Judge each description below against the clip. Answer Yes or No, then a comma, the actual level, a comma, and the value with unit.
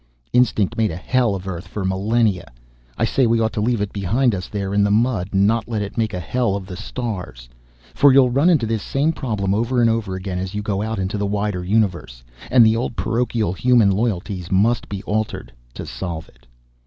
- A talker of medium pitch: No, low, 105 Hz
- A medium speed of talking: No, fast, 220 wpm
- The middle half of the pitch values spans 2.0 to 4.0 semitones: Yes, average, 3.5 semitones